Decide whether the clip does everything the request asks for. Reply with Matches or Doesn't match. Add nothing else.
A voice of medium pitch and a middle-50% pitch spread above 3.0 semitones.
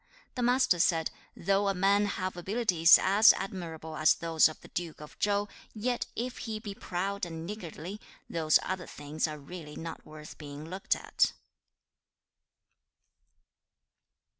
Matches